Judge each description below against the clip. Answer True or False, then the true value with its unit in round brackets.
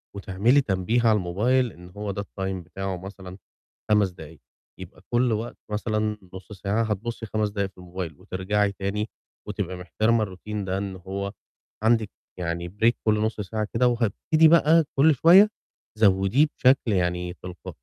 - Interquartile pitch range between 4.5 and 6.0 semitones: False (3.3 semitones)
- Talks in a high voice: False (100 Hz)